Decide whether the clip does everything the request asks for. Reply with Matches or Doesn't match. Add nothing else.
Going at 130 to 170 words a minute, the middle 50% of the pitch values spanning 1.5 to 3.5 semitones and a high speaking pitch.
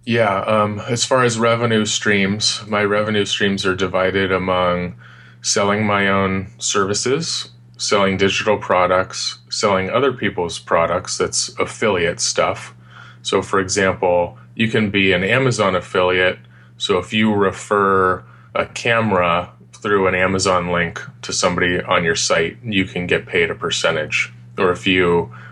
Doesn't match